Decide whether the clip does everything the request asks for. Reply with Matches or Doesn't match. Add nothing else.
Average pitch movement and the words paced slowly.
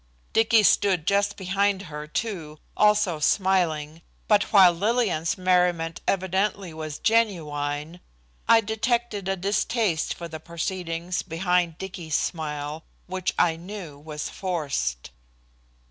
Matches